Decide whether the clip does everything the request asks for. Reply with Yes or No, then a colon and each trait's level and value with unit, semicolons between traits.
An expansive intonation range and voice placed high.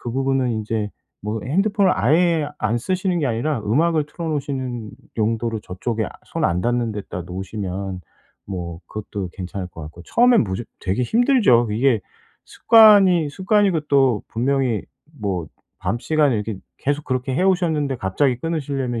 No: wide, 6.7 semitones; low, 125 Hz